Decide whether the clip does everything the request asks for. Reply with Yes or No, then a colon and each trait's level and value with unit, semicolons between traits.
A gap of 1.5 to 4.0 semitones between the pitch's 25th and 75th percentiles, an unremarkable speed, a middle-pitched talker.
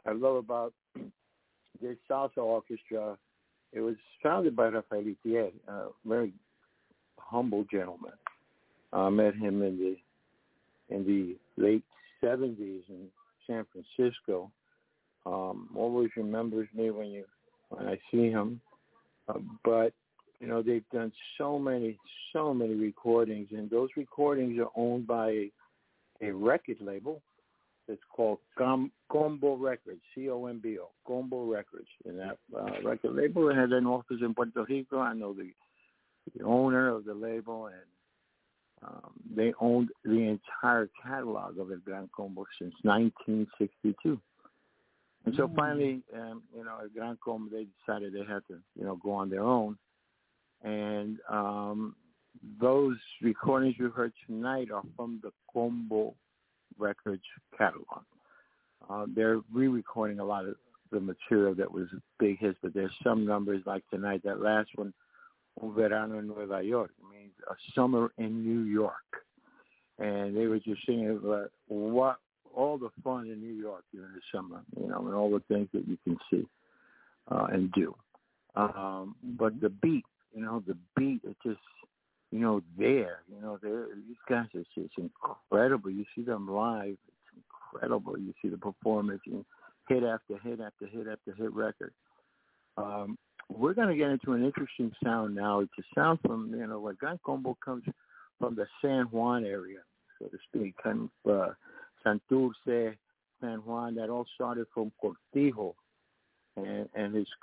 No: average, 2.9 semitones; average, 155 wpm; low, 110 Hz